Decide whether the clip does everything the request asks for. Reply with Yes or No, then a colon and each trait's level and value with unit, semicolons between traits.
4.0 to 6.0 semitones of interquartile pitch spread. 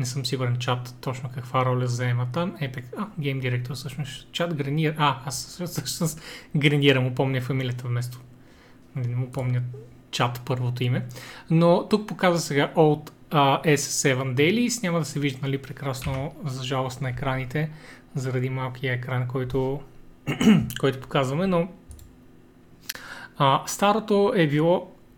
No: average, 3.3 semitones